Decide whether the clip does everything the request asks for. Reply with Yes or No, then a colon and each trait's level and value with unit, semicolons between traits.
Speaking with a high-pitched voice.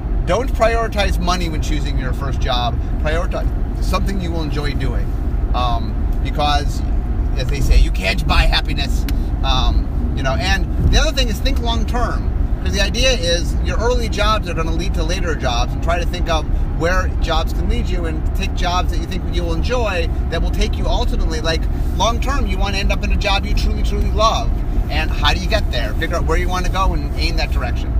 No: very low, 70 Hz